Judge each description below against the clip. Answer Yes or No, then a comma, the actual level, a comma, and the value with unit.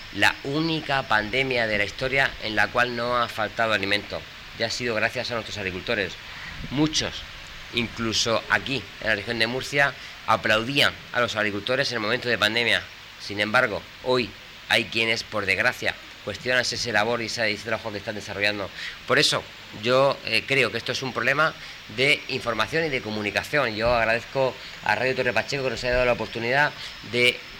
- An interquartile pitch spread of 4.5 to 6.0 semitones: No, average, 3.3 semitones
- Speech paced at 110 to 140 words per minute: No, average, 175 wpm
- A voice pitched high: No, low, 115 Hz